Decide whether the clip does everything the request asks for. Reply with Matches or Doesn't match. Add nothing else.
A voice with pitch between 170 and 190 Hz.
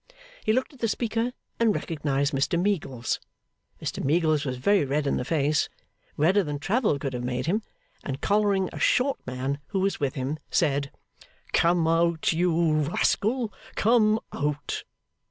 Doesn't match